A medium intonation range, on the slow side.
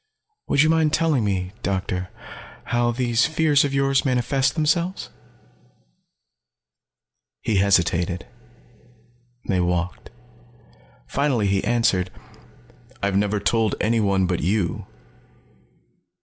No: wide, 6.4 semitones; slow, 95 wpm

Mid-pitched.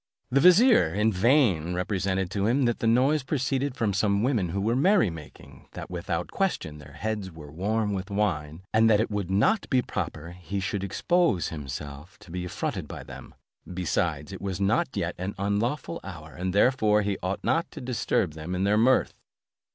No: low, 100 Hz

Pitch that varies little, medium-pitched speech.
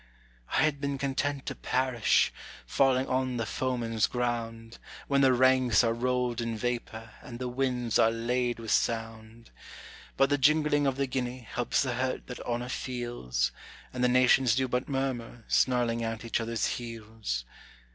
No: narrow, 2.1 semitones; low, 125 Hz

